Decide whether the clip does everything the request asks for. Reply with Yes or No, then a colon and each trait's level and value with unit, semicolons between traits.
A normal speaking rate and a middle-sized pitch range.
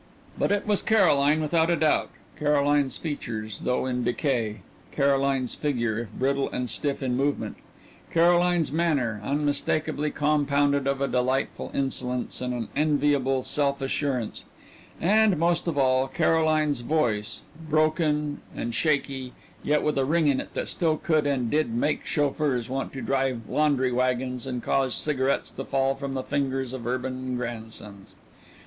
Yes: average, 150 wpm; average, 3.0 semitones